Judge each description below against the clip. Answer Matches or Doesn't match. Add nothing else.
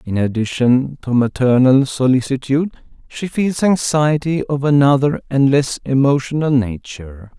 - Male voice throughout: Matches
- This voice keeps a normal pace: Doesn't match